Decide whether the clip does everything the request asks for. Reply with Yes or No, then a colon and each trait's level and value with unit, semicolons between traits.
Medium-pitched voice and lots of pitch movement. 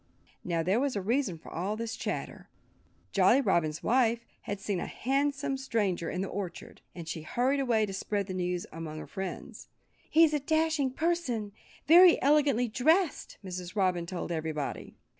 No: high, 215 Hz; wide, 7.3 semitones